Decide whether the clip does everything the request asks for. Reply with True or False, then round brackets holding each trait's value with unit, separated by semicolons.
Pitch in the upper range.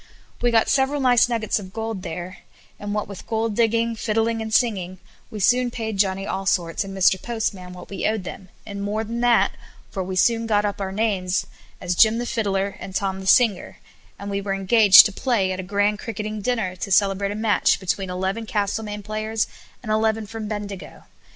True (210 Hz)